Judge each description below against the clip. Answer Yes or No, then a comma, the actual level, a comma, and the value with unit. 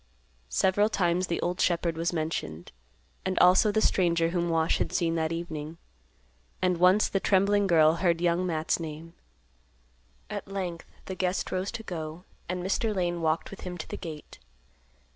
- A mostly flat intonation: Yes, narrow, 2.1 semitones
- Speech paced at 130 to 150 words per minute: No, average, 165 wpm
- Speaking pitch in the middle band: Yes, medium, 175 Hz